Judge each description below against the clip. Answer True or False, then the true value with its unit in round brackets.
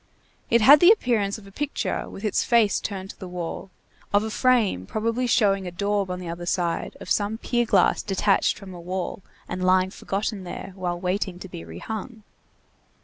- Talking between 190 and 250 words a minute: True (195 wpm)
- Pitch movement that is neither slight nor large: True (3.3 semitones)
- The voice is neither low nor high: False (195 Hz)